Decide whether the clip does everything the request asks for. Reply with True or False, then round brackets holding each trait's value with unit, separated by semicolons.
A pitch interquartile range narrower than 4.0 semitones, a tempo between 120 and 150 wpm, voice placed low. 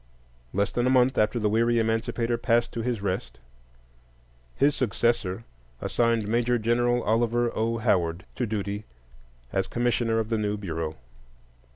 True (2.5 semitones; 145 wpm; 115 Hz)